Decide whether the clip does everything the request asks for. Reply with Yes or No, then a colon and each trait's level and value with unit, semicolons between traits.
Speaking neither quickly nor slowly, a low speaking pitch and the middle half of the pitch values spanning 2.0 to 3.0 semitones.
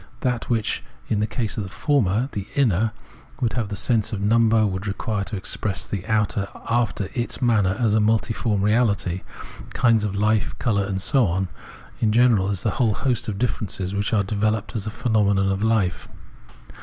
Yes: average, 180 wpm; low, 105 Hz; narrow, 2.4 semitones